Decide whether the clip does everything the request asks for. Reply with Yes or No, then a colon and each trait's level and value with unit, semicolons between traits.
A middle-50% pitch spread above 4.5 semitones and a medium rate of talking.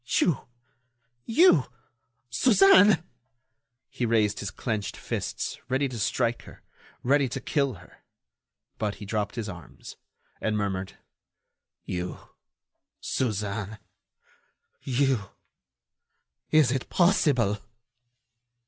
No: average, 5.2 semitones; slow, 95 wpm